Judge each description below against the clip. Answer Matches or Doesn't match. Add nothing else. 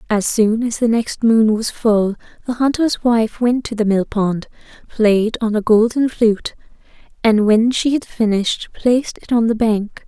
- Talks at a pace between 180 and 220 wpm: Matches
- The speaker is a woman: Matches